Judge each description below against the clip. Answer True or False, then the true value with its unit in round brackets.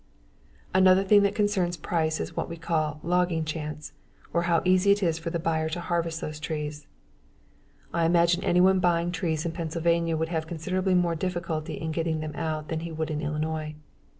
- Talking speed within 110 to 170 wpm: False (185 wpm)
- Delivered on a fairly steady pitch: True (1.9 semitones)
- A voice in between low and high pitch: True (165 Hz)